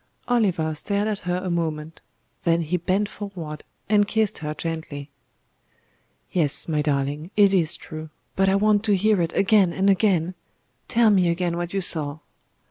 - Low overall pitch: No, medium, 175 Hz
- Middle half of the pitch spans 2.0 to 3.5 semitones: No, average, 4.1 semitones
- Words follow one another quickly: No, average, 165 wpm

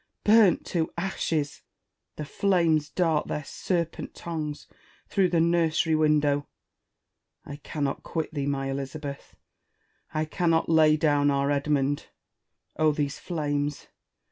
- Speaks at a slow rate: Yes, slow, 115 wpm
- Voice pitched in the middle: Yes, medium, 155 Hz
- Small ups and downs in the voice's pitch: Yes, narrow, 2.3 semitones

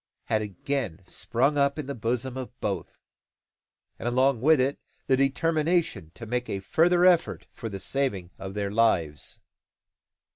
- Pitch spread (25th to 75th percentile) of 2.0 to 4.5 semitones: No, average, 5.2 semitones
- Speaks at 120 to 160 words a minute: Yes, average, 150 wpm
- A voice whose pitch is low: Yes, low, 125 Hz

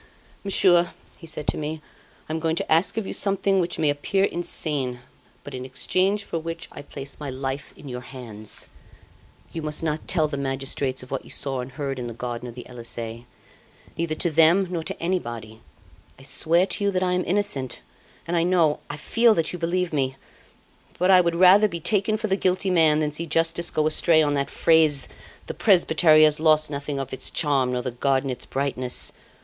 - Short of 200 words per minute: No, fast, 205 wpm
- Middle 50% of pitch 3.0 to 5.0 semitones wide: Yes, average, 4.5 semitones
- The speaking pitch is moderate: Yes, medium, 155 Hz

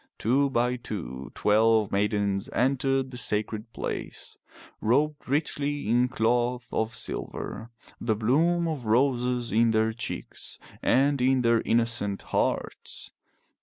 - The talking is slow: Yes, slow, 120 wpm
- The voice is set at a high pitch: No, low, 120 Hz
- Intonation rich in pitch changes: No, average, 3.3 semitones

